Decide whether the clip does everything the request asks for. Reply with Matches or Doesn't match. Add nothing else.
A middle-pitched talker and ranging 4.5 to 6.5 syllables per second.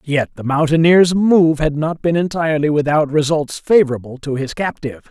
Matches